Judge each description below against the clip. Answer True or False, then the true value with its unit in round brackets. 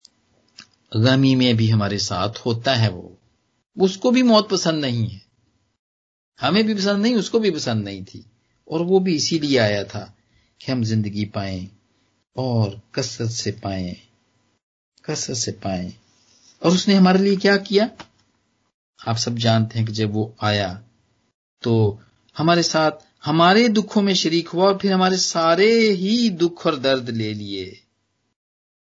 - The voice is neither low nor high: False (120 Hz)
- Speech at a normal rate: True (155 wpm)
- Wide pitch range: True (8.2 semitones)